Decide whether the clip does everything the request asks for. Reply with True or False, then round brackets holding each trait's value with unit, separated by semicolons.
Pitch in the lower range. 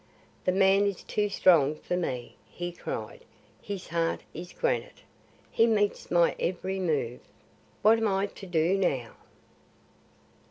False (185 Hz)